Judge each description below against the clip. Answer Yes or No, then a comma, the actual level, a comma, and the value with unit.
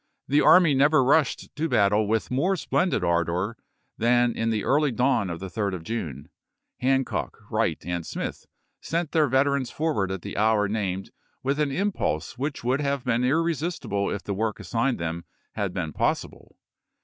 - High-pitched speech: No, low, 120 Hz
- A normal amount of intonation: No, wide, 6.2 semitones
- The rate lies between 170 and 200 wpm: Yes, average, 175 wpm